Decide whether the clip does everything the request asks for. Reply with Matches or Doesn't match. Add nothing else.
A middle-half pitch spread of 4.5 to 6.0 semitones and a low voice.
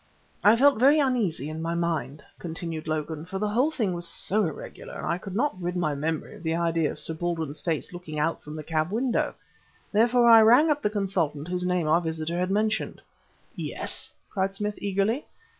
Doesn't match